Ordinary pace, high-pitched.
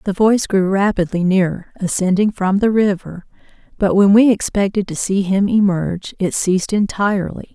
Yes: average, 160 wpm; high, 195 Hz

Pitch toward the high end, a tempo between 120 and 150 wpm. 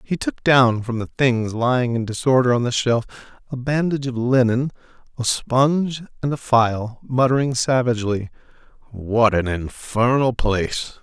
No: low, 120 Hz; average, 145 wpm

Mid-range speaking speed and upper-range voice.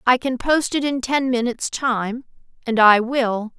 Yes: average, 165 wpm; high, 245 Hz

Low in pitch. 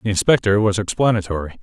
Yes: low, 100 Hz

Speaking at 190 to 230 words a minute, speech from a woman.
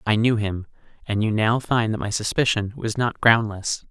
No: average, 200 wpm; male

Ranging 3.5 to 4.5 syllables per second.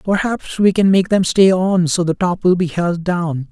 Yes: 4.4 syllables/s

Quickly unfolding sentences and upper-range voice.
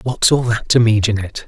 No: fast, 245 wpm; low, 115 Hz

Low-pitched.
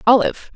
No: high, 225 Hz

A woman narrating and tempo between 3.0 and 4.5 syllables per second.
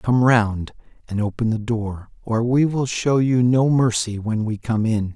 No: male; 4.1 syllables/s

